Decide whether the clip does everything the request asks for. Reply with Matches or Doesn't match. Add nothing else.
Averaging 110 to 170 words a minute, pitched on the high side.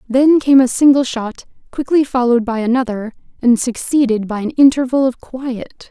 Matches